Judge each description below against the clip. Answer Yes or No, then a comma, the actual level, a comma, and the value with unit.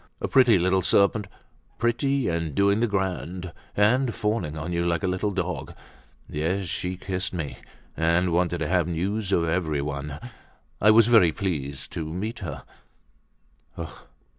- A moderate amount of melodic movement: Yes, average, 3.9 semitones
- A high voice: No, very low, 90 Hz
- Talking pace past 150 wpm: No, average, 140 wpm